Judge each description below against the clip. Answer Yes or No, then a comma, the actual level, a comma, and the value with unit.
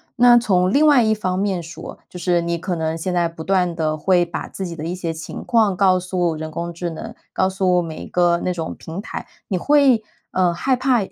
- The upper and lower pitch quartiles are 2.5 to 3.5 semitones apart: Yes, average, 2.9 semitones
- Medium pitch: Yes, medium, 180 Hz